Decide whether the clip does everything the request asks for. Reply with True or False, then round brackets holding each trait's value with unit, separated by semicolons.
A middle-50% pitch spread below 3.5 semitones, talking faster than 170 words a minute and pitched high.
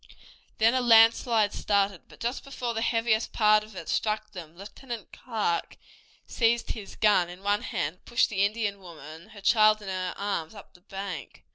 True (3.1 semitones; 180 wpm; 210 Hz)